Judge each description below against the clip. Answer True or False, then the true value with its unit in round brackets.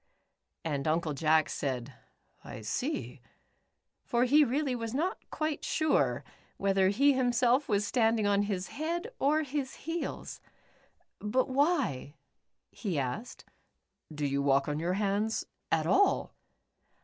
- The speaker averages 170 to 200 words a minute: False (135 wpm)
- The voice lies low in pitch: False (220 Hz)